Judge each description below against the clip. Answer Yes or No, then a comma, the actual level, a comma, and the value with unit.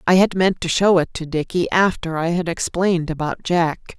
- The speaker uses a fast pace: Yes, fast, 210 wpm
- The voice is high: No, medium, 170 Hz